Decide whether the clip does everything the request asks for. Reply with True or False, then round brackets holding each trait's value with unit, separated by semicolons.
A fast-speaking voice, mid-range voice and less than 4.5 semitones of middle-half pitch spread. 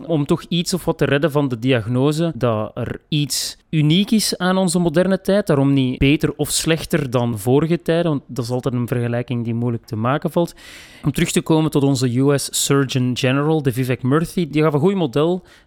False (210 wpm; 145 Hz; 4.8 semitones)